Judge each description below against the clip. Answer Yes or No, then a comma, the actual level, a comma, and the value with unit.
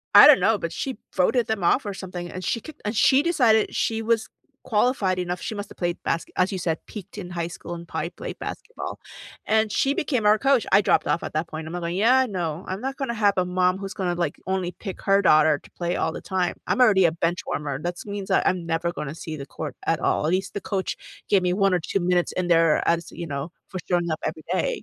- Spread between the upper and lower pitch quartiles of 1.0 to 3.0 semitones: No, average, 3.9 semitones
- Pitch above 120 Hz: Yes, medium, 185 Hz